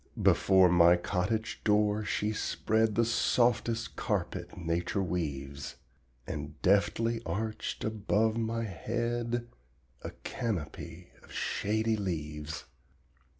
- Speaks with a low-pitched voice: Yes, low, 105 Hz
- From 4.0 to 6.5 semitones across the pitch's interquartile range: Yes, average, 4.5 semitones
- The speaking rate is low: Yes, slow, 100 wpm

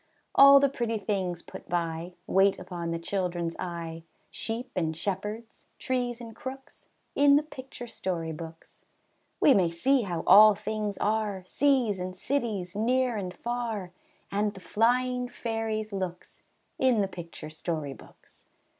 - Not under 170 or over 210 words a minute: No, average, 145 wpm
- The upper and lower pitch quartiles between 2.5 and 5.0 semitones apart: No, wide, 5.4 semitones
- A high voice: Yes, high, 205 Hz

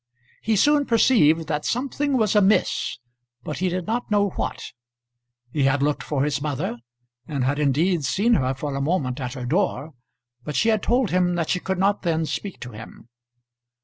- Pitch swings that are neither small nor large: No, wide, 6.4 semitones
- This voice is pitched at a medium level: Yes, medium, 165 Hz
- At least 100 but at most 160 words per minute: No, average, 185 wpm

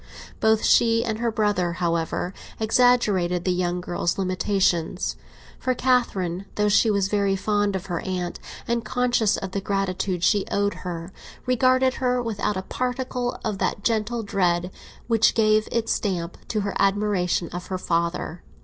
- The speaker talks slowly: No, average, 155 wpm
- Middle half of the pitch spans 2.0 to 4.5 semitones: Yes, average, 3.9 semitones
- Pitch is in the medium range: No, high, 200 Hz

